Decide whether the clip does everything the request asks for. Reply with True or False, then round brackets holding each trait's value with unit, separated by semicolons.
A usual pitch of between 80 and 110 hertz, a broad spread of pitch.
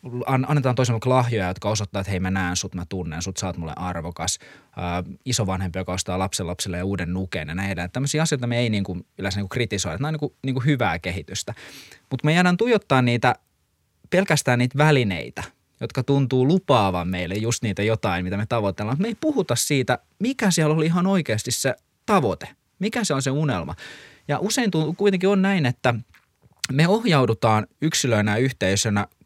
False (120 Hz; 7.6 semitones)